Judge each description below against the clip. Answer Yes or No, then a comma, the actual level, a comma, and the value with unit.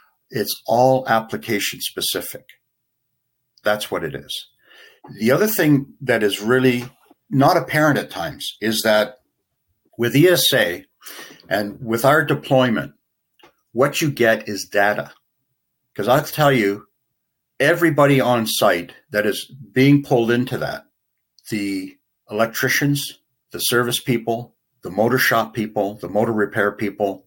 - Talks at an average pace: No, slow, 125 wpm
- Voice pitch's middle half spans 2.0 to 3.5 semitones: No, average, 3.9 semitones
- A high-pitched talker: No, low, 125 Hz